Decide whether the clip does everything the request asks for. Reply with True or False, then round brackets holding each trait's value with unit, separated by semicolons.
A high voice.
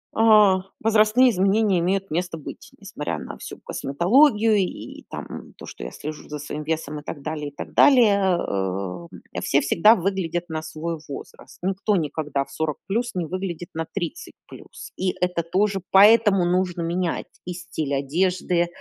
False (180 Hz)